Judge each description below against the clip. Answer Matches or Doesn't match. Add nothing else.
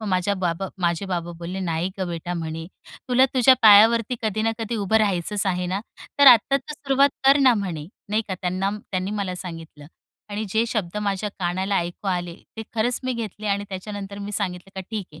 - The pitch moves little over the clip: Doesn't match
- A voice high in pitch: Matches